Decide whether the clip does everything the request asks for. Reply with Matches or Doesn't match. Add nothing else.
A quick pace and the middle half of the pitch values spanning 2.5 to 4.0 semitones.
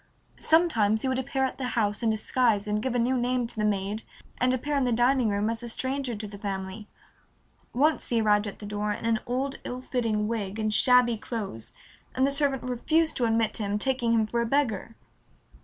Matches